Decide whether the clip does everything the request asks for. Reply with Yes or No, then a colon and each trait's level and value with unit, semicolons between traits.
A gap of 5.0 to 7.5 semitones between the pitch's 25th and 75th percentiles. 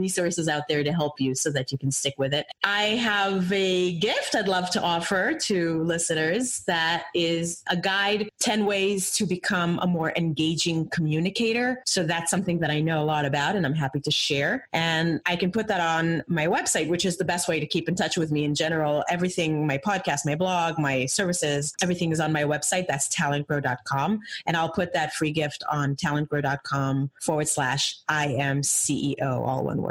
No: average, 3.8 semitones